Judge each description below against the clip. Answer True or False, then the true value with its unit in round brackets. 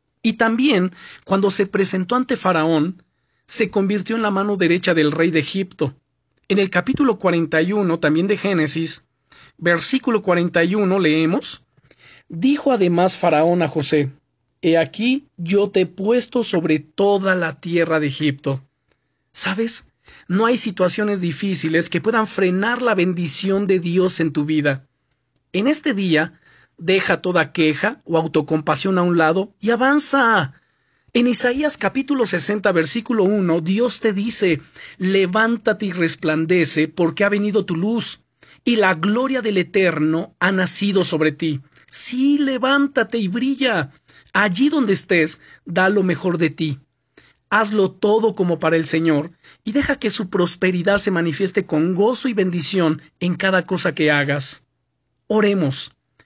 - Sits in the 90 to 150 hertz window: False (185 Hz)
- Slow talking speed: False (140 wpm)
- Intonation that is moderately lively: True (4.7 semitones)